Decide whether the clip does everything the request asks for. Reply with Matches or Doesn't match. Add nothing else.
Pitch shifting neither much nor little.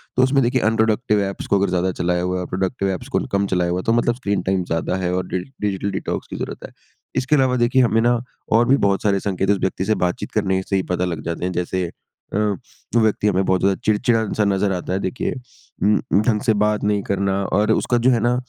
Matches